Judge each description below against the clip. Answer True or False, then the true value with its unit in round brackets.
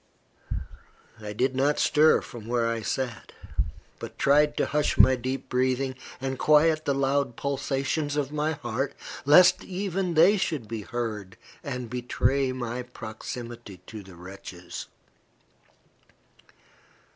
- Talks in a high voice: False (130 Hz)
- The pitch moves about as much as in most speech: True (3.8 semitones)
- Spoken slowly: True (125 wpm)